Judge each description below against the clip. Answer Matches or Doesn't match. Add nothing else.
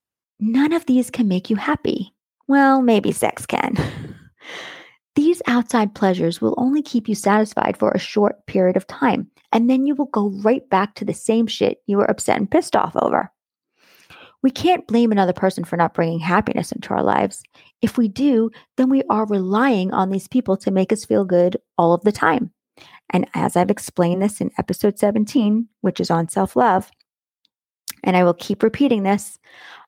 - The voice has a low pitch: Doesn't match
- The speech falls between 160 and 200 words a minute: Matches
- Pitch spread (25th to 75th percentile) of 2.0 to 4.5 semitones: Doesn't match